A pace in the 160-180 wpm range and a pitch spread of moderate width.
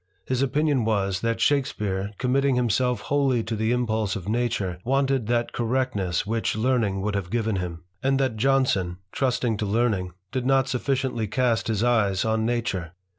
Yes: average, 165 wpm; average, 4.0 semitones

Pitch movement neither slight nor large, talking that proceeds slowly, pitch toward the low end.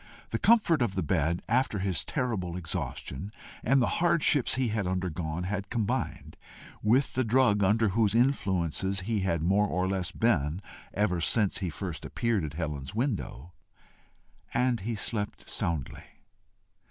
No: average, 4.9 semitones; average, 145 wpm; low, 100 Hz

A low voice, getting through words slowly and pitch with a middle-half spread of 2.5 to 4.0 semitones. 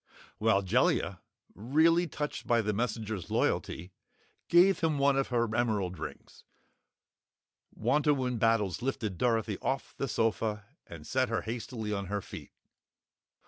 No: low, 115 Hz; slow, 130 wpm; average, 4.4 semitones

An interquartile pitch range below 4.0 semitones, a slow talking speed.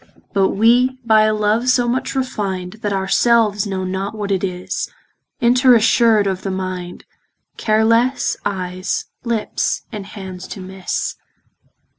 No: average, 3.5 semitones; average, 145 wpm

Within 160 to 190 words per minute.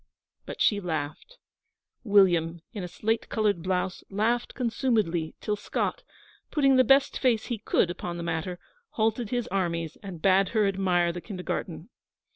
No: average, 150 wpm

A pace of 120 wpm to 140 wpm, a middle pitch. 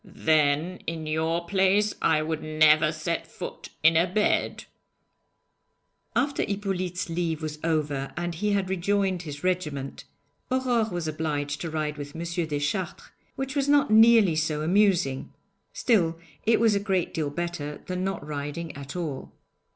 No: average, 150 wpm; medium, 170 Hz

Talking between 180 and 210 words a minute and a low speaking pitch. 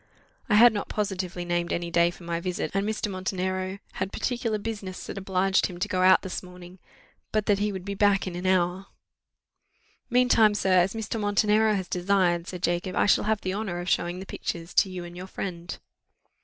No: fast, 205 wpm; medium, 185 Hz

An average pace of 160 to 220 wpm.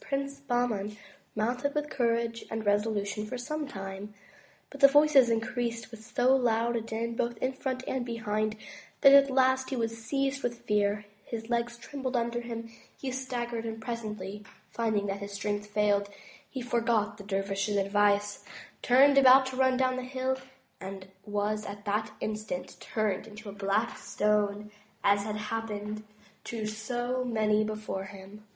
Yes: average, 165 wpm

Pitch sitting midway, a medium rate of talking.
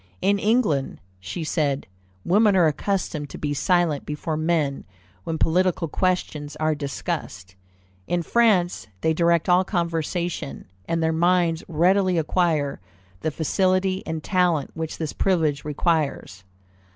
No: medium, 165 Hz; slow, 125 wpm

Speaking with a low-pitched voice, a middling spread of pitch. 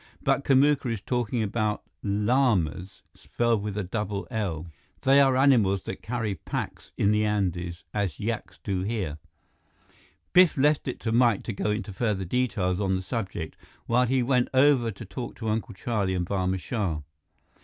Yes: low, 105 Hz; average, 4.4 semitones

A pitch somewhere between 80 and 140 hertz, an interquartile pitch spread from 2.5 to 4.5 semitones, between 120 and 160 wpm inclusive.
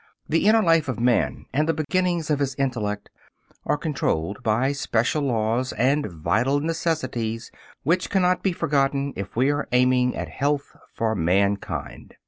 No: low, 135 Hz; average, 5.0 semitones; average, 150 wpm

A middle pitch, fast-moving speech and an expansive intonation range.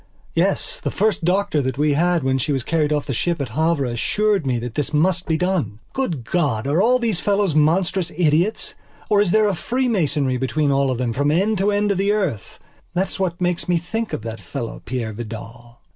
Yes: medium, 160 Hz; fast, 220 wpm; wide, 6.5 semitones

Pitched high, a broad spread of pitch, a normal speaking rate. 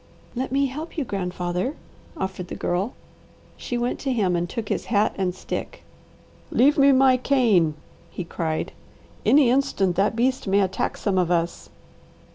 Yes: high, 210 Hz; wide, 6.3 semitones; average, 160 wpm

